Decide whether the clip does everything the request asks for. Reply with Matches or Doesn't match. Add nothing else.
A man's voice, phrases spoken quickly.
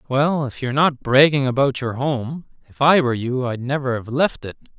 Matches